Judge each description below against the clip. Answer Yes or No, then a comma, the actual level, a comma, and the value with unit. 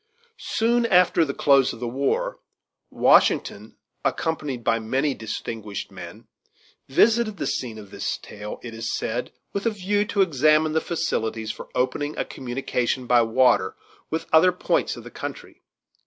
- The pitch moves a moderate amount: No, wide, 7.6 semitones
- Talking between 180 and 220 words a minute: No, average, 155 wpm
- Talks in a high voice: No, low, 135 Hz